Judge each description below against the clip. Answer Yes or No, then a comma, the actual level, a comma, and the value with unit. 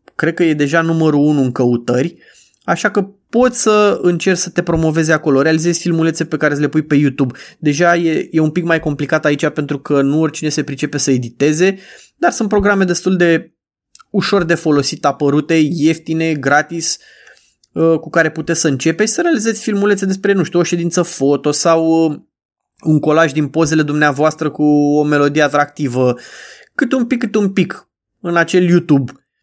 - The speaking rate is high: Yes, fast, 175 wpm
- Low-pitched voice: No, medium, 160 Hz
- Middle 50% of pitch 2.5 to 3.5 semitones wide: Yes, average, 3.0 semitones